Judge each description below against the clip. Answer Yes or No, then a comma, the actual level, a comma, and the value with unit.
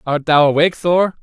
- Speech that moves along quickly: No, average, 195 wpm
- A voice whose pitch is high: No, medium, 160 Hz